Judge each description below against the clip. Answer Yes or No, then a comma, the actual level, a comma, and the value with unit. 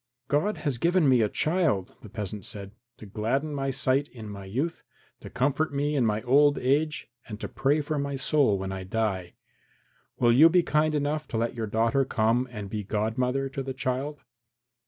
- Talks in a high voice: No, low, 130 Hz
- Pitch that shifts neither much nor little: Yes, average, 5.0 semitones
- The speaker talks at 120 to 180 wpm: No, average, 195 wpm